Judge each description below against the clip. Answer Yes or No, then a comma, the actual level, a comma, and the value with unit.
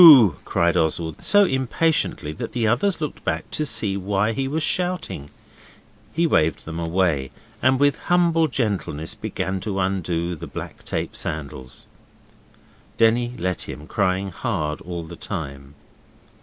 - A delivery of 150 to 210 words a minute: No, average, 140 wpm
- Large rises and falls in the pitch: Yes, wide, 8.3 semitones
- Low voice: Yes, very low, 95 Hz